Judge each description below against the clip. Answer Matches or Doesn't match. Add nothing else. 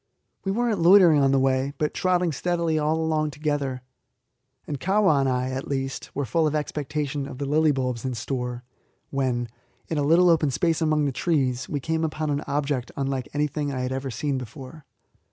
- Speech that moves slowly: Doesn't match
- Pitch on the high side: Doesn't match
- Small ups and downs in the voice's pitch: Doesn't match